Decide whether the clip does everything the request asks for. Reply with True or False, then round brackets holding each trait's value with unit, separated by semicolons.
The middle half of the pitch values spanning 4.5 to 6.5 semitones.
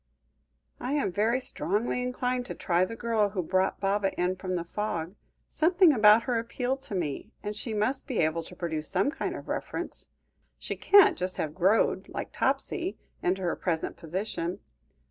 True (5.5 semitones)